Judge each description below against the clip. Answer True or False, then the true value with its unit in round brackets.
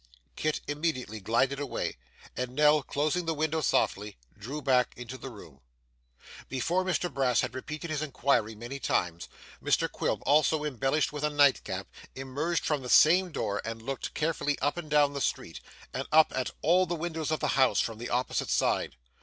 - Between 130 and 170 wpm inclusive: False (180 wpm)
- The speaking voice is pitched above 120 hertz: True (140 Hz)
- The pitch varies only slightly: False (3.6 semitones)